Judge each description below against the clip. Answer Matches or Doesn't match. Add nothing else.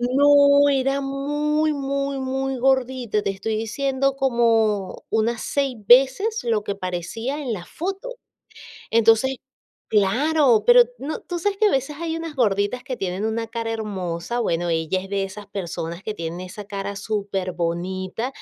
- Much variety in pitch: Matches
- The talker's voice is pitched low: Doesn't match